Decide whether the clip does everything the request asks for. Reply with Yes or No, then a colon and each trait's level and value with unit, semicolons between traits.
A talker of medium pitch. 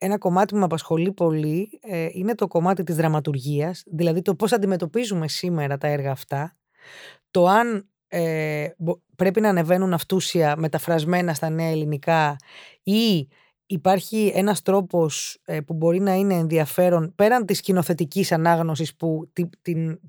Yes: medium, 170 Hz